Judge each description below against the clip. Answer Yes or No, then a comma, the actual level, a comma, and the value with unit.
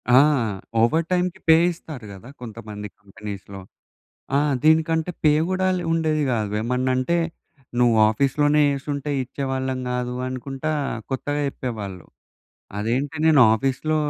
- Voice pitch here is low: Yes, low, 130 Hz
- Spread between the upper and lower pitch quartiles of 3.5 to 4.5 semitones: No, average, 4.9 semitones